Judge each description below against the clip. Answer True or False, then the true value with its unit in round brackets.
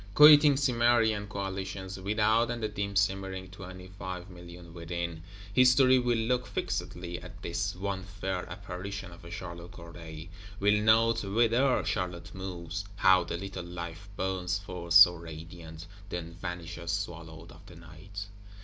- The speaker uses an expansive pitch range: False (2.9 semitones)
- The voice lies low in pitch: True (95 Hz)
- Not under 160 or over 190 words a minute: False (140 wpm)